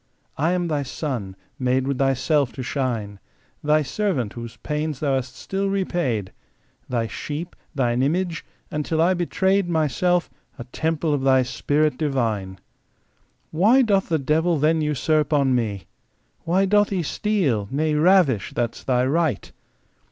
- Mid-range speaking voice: Yes, medium, 150 Hz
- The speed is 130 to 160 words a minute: Yes, average, 140 wpm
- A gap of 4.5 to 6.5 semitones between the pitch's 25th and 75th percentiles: Yes, average, 5.1 semitones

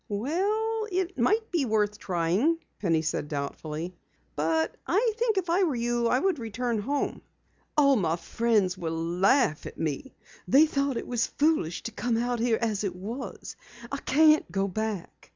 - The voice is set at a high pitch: Yes, high, 235 Hz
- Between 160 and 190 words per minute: Yes, average, 170 wpm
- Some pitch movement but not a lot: No, wide, 8.7 semitones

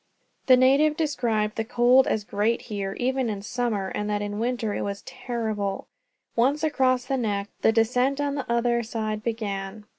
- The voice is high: Yes, high, 230 Hz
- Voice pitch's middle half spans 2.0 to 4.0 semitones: Yes, average, 3.5 semitones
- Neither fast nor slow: Yes, average, 175 wpm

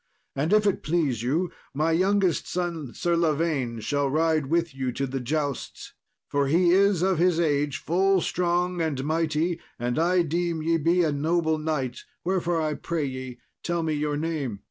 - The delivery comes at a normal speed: Yes, average, 175 wpm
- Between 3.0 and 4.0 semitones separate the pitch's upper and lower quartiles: Yes, average, 3.3 semitones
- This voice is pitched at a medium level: Yes, medium, 160 Hz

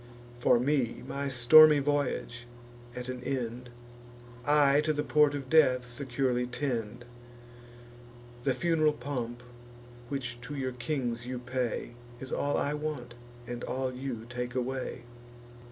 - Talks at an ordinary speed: No, slow, 130 wpm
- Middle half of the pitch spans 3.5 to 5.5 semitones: No, average, 2.8 semitones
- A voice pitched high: No, low, 130 Hz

